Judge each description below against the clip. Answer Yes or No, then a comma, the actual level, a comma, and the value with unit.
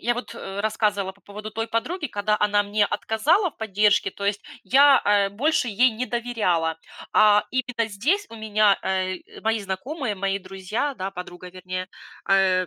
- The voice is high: Yes, high, 210 Hz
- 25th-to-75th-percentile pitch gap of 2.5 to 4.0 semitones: Yes, average, 3.3 semitones